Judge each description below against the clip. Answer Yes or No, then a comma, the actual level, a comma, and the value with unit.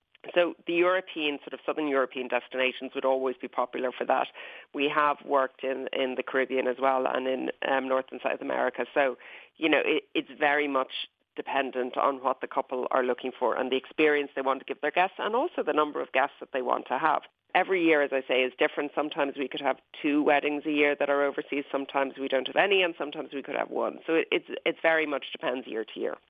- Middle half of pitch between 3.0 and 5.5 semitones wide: No, narrow, 2.5 semitones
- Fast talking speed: Yes, fast, 235 wpm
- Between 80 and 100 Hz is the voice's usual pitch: No, medium, 140 Hz